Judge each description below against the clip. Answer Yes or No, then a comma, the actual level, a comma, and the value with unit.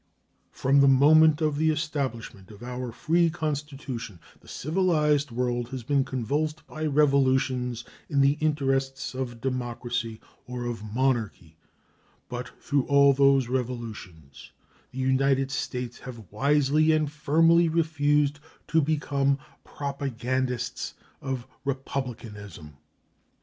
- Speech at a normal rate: No, slow, 115 wpm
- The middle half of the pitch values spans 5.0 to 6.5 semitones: No, average, 3.3 semitones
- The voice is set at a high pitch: No, low, 135 Hz